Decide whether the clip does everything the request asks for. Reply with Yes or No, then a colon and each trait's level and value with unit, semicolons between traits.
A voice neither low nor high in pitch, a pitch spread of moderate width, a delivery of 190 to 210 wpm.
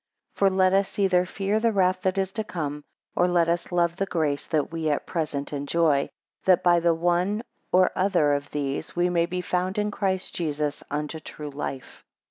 Yes: medium, 175 Hz; average, 3.8 semitones; average, 200 wpm